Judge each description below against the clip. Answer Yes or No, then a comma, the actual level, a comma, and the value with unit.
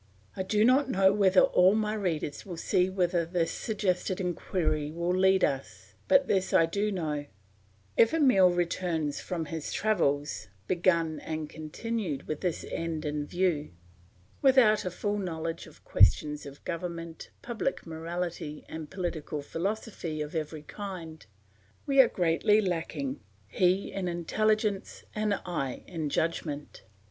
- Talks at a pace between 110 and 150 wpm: Yes, average, 140 wpm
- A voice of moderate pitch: Yes, medium, 175 Hz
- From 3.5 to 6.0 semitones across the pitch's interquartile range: Yes, average, 3.8 semitones